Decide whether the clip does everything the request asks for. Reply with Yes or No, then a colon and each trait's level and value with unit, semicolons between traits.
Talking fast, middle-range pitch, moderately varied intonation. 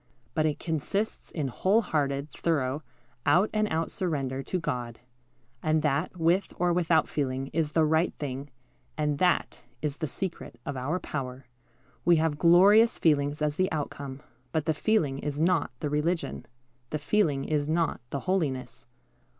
No: average, 160 wpm; medium, 155 Hz; average, 3.4 semitones